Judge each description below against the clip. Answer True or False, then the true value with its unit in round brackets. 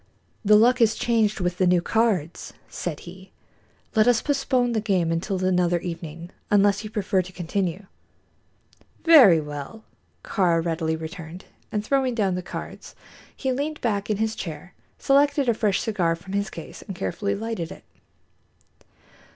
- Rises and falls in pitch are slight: False (4.3 semitones)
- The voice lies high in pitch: True (195 Hz)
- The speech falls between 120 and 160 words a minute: True (155 wpm)